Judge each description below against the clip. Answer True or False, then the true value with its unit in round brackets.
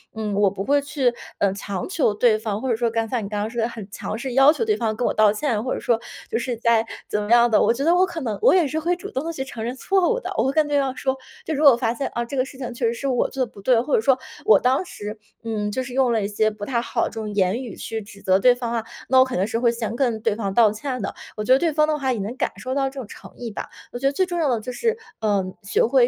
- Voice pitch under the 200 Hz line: False (240 Hz)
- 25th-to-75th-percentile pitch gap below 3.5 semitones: False (3.8 semitones)